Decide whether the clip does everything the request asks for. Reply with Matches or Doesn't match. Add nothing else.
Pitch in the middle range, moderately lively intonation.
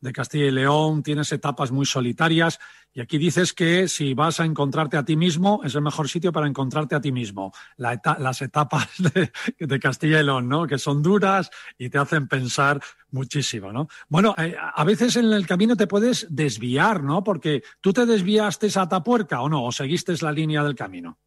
Matches